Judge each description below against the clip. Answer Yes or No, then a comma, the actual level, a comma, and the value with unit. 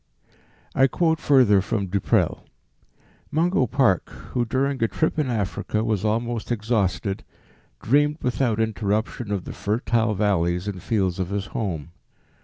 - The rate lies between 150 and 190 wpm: No, average, 140 wpm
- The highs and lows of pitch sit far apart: No, average, 4.1 semitones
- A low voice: Yes, low, 110 Hz